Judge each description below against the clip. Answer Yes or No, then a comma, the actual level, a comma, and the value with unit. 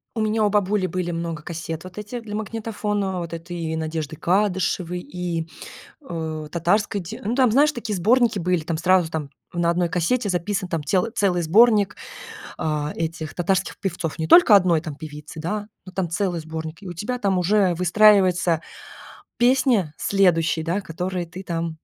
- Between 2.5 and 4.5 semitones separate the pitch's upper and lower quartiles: Yes, average, 3.9 semitones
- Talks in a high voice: No, medium, 180 Hz